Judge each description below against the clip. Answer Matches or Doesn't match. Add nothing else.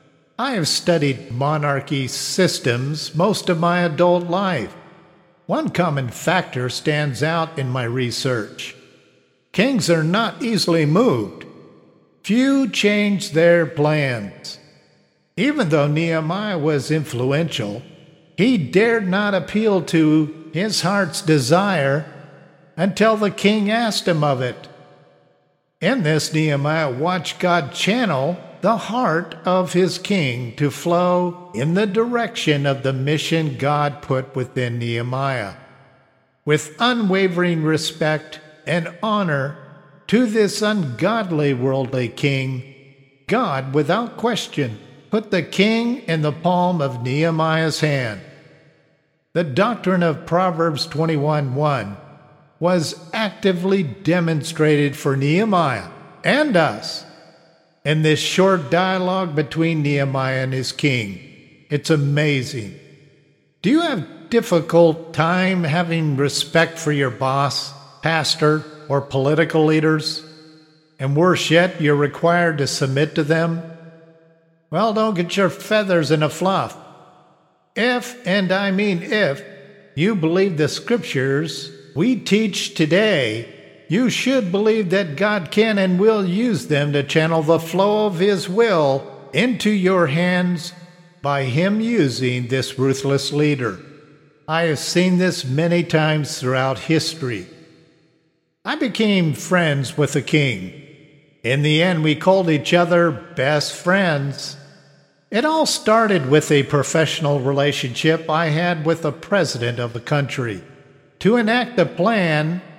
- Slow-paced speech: Matches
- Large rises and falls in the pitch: Doesn't match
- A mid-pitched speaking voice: Matches